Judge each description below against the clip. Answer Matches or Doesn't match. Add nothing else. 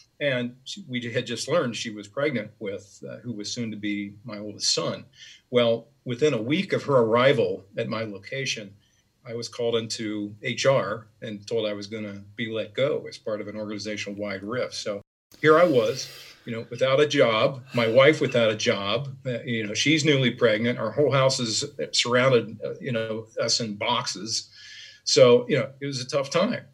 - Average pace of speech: Matches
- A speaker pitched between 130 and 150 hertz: Doesn't match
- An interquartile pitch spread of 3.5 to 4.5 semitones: Matches